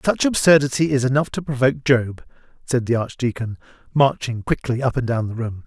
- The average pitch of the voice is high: No, low, 130 Hz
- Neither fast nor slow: Yes, average, 180 wpm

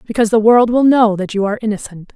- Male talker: No, female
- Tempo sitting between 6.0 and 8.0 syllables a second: Yes, 7.0 syllables/s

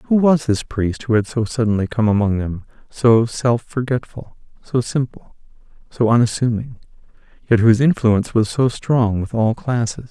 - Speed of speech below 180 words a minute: Yes, average, 160 wpm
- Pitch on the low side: Yes, low, 115 Hz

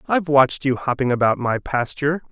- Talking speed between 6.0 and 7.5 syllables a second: Yes, 6.2 syllables/s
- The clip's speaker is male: Yes, male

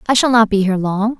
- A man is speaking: No, female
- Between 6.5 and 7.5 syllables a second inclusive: Yes, 6.8 syllables/s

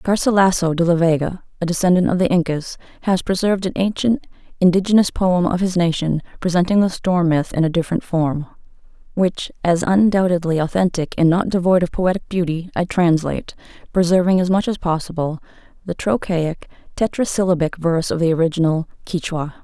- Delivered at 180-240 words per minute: No, average, 155 wpm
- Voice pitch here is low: No, medium, 175 Hz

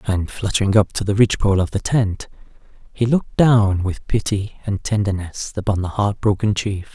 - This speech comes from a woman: No, male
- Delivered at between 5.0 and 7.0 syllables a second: Yes, 5.2 syllables/s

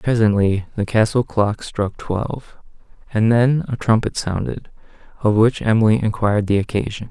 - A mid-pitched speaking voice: No, low, 110 Hz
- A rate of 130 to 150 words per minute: Yes, average, 145 wpm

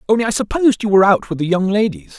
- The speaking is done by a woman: No, male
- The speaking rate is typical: No, fast, 275 wpm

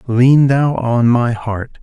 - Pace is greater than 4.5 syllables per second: No, 3.0 syllables/s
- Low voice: Yes, low, 125 Hz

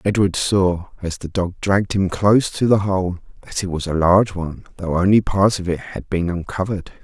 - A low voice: Yes, very low, 95 Hz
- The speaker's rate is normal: No, fast, 215 wpm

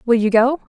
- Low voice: No, high, 240 Hz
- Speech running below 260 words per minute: Yes, fast, 235 wpm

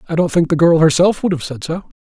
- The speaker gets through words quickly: Yes, fast, 295 wpm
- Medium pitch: Yes, medium, 165 Hz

